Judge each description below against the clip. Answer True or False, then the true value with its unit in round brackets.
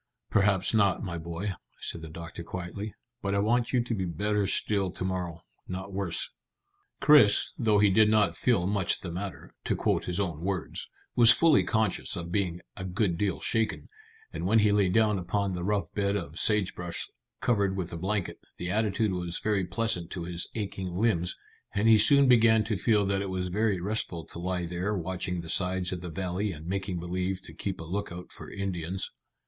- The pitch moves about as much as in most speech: True (3.0 semitones)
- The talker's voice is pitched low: True (95 Hz)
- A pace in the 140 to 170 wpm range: False (195 wpm)